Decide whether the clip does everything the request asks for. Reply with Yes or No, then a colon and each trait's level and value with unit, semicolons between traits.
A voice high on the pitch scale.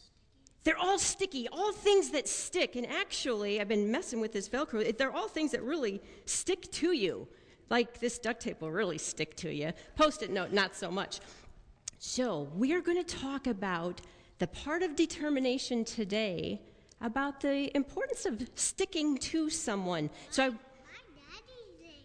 Yes: very high, 265 Hz